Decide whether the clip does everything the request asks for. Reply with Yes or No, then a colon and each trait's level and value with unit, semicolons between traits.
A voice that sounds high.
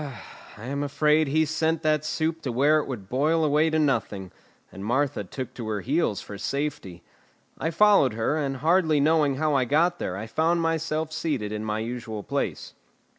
No: medium, 145 Hz